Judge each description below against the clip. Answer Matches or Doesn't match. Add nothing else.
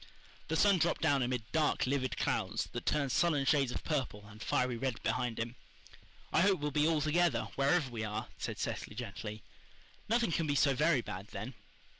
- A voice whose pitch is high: Doesn't match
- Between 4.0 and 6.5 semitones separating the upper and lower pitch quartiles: Matches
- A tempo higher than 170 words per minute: Matches